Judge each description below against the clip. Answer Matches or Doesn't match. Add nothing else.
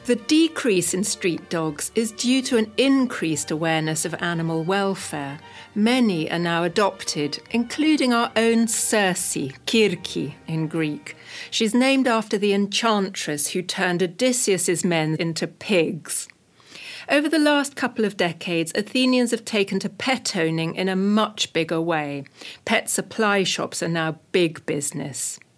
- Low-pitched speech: Doesn't match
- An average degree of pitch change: Doesn't match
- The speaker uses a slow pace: Doesn't match